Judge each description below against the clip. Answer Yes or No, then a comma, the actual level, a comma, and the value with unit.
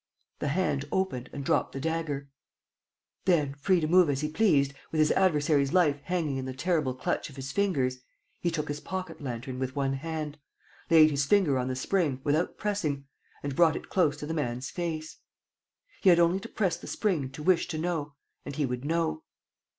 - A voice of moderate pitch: Yes, medium, 150 Hz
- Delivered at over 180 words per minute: Yes, average, 195 wpm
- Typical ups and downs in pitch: Yes, average, 3.8 semitones